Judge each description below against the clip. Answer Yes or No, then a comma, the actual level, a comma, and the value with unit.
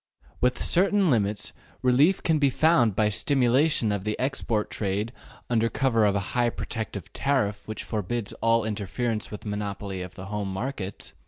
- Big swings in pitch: No, average, 3.8 semitones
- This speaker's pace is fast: No, average, 160 wpm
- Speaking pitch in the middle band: No, low, 110 Hz